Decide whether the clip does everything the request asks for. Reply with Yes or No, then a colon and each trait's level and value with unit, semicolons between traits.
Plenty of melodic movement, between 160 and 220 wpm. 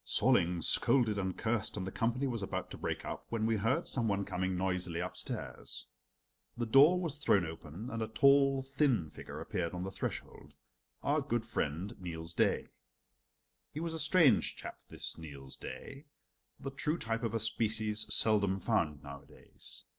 Yes: wide, 6.4 semitones; average, 170 wpm